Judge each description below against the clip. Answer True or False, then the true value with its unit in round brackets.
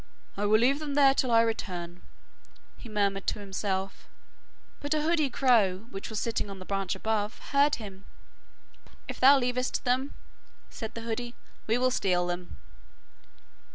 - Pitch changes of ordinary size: True (4.6 semitones)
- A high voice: True (225 Hz)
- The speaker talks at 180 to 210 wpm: False (155 wpm)